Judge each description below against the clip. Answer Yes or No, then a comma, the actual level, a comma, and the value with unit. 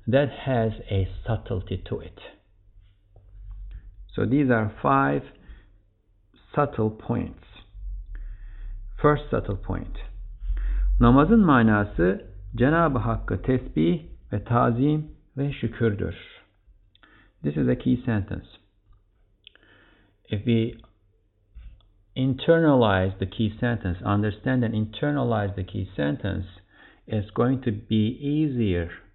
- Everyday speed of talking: No, slow, 95 wpm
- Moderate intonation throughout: Yes, average, 3.7 semitones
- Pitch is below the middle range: Yes, low, 105 Hz